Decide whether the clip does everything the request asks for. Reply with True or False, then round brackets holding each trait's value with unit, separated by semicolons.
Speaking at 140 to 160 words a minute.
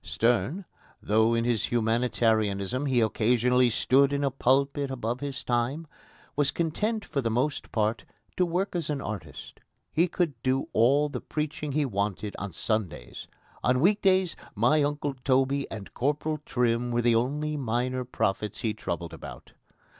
True (155 wpm)